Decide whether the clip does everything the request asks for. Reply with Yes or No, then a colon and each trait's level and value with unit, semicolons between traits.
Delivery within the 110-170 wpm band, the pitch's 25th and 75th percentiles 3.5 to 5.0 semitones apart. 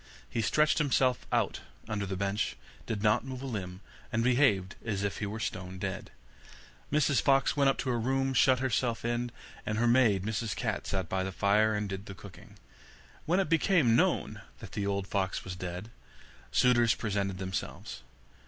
No: average, 180 wpm; average, 4.5 semitones